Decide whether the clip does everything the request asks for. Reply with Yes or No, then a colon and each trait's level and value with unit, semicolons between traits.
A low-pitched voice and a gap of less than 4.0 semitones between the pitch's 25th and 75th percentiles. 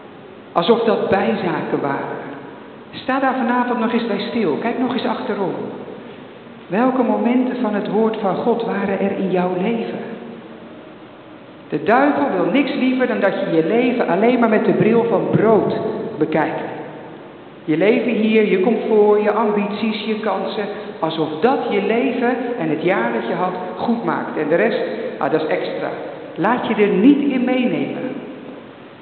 No: high, 220 Hz; average, 3.3 semitones